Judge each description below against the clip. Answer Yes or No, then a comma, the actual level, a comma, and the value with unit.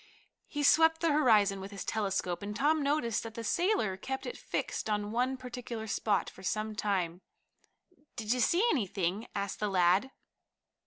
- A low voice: No, high, 220 Hz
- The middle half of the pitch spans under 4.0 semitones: No, average, 5.1 semitones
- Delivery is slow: No, average, 165 wpm